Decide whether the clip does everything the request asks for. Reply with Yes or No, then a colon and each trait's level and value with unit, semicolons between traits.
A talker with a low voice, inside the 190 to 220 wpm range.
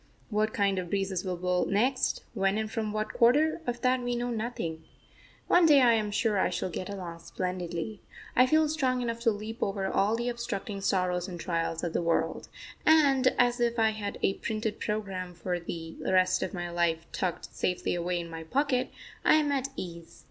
No: high, 205 Hz; average, 200 wpm